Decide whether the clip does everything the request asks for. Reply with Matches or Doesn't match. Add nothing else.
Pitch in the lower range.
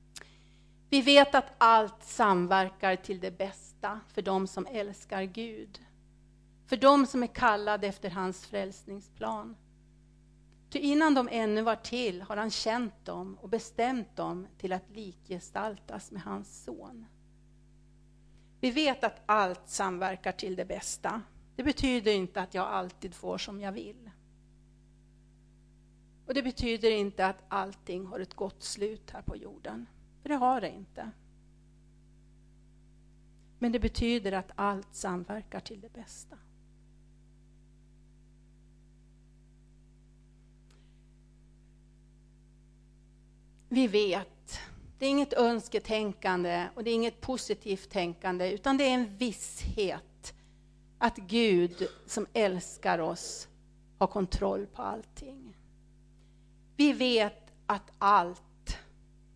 Doesn't match